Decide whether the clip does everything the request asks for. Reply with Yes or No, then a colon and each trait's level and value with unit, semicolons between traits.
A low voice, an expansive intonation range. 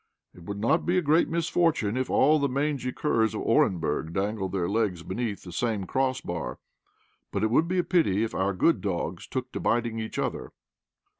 Yes: low, 115 Hz; wide, 6.8 semitones